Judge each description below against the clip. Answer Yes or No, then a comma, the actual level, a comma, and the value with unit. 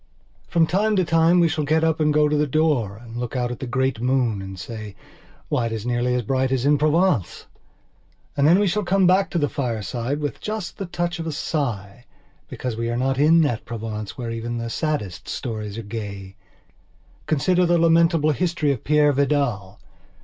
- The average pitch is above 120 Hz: Yes, low, 135 Hz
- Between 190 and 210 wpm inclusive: Yes, average, 200 wpm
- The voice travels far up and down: Yes, wide, 5.8 semitones